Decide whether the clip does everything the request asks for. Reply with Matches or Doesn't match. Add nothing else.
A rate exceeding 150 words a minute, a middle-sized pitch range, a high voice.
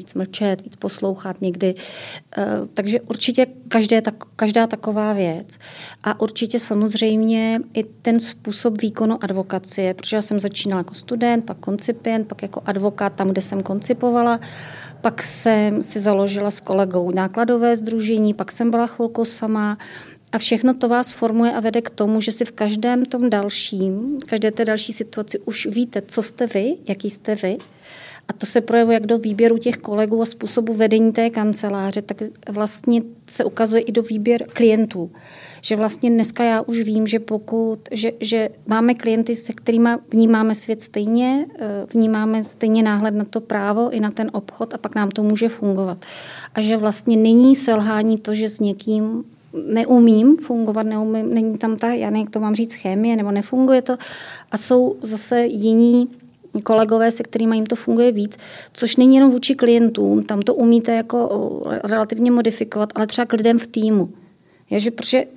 Doesn't match